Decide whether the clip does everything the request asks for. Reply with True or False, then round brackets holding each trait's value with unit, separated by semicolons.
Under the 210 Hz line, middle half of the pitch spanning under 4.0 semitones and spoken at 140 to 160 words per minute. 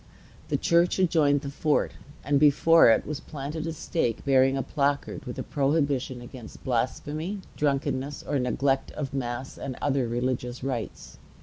True (140 Hz; 2.5 semitones; 150 wpm)